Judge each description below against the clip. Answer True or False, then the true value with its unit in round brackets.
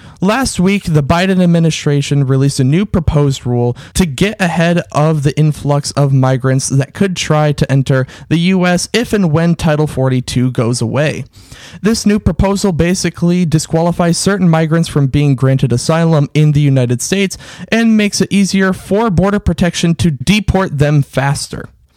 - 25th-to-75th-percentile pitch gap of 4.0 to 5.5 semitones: True (5.1 semitones)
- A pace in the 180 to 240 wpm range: False (160 wpm)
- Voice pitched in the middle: True (160 Hz)